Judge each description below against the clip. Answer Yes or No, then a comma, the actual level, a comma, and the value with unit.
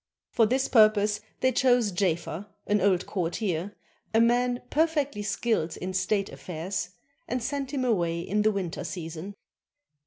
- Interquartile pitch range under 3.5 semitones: No, average, 5.0 semitones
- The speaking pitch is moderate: No, high, 205 Hz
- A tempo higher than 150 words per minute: No, average, 145 wpm